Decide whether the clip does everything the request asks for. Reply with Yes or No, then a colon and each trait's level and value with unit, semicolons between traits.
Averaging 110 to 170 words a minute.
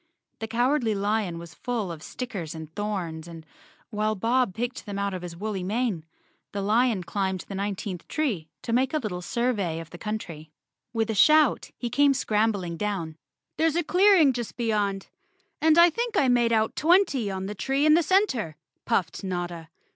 No: average, 180 wpm